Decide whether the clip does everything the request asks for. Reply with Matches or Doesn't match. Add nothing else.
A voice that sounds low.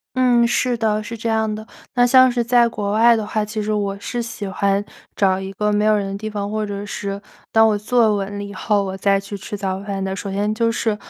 Doesn't match